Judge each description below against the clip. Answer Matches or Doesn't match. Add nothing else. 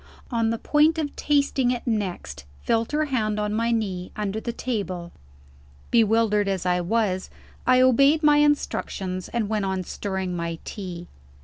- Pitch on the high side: Matches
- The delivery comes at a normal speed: Matches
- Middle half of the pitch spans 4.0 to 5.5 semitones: Matches